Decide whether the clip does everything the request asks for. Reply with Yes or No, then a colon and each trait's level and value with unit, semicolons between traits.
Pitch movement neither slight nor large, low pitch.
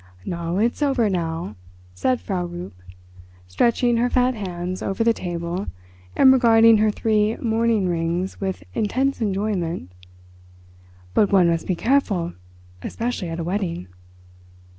No: average, 5.0 semitones; high, 195 Hz